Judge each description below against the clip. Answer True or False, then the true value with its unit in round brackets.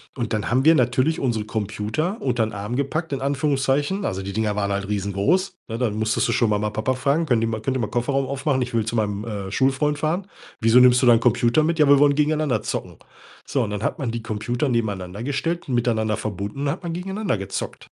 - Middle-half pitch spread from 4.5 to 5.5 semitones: True (4.9 semitones)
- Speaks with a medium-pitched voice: False (120 Hz)